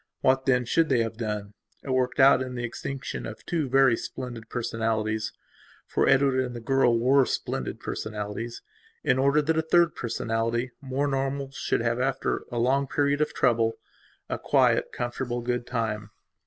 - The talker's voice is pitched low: Yes, low, 125 Hz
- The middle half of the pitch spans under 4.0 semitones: Yes, average, 2.8 semitones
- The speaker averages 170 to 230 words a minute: No, average, 160 wpm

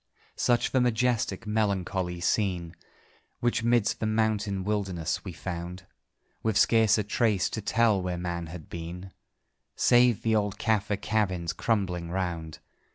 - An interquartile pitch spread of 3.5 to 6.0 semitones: Yes, average, 3.8 semitones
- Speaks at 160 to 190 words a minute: No, slow, 135 wpm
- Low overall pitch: Yes, low, 100 Hz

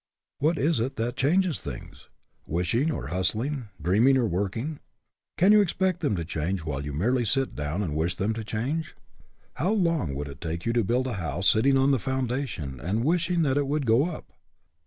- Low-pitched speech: Yes, low, 120 Hz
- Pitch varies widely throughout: Yes, wide, 8.4 semitones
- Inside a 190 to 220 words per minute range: Yes, average, 200 wpm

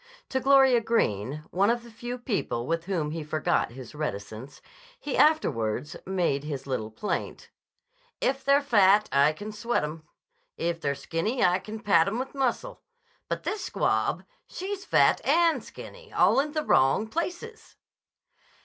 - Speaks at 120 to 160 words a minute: Yes, average, 155 wpm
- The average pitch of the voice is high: Yes, high, 205 Hz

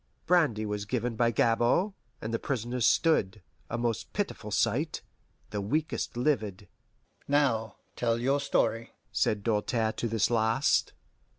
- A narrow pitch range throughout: No, average, 3.9 semitones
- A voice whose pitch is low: Yes, low, 115 Hz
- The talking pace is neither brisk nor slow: No, slow, 130 wpm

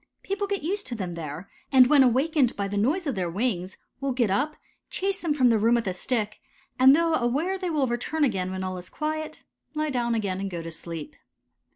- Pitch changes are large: Yes, wide, 7.9 semitones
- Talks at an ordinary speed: No, fast, 225 wpm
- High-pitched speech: Yes, high, 245 Hz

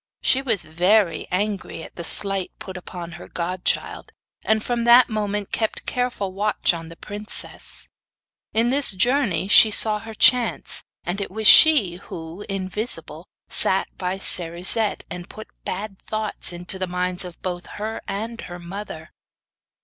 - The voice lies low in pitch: No, high, 195 Hz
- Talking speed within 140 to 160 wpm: Yes, average, 150 wpm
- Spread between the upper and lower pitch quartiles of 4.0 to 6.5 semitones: No, average, 3.5 semitones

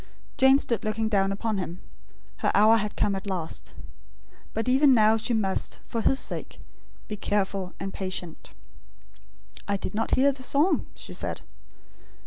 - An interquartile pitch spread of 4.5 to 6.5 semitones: No, average, 3.6 semitones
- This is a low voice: No, high, 215 Hz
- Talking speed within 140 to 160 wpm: Yes, average, 155 wpm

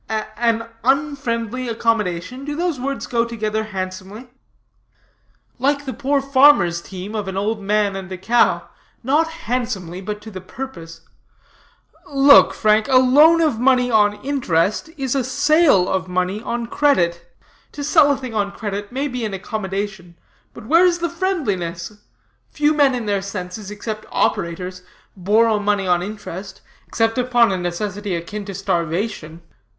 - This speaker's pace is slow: No, average, 150 wpm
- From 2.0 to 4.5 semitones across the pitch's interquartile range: No, wide, 5.6 semitones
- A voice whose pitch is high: Yes, high, 215 Hz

